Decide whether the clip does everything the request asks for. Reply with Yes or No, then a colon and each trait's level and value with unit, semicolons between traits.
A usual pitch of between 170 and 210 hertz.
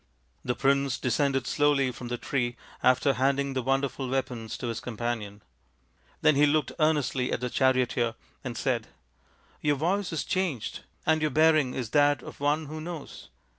No: low, 135 Hz